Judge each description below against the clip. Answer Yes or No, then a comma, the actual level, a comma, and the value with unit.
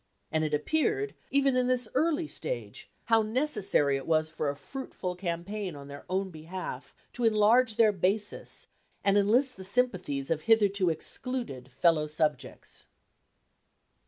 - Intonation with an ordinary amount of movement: No, wide, 7.9 semitones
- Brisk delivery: No, average, 140 wpm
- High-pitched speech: Yes, high, 200 Hz